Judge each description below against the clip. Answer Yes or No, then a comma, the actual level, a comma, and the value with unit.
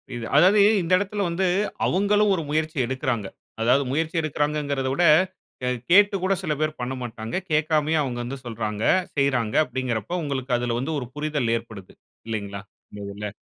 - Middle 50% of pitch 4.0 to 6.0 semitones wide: Yes, average, 5.2 semitones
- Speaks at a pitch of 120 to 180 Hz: Yes, medium, 140 Hz